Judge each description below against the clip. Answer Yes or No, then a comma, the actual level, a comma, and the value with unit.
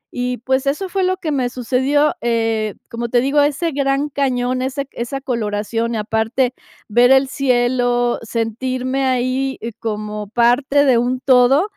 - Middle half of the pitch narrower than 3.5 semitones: Yes, narrow, 2.5 semitones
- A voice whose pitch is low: No, very high, 250 Hz